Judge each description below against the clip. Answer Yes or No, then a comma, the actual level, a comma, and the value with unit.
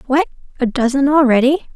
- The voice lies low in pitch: No, very high, 270 Hz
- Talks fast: No, slow, 135 wpm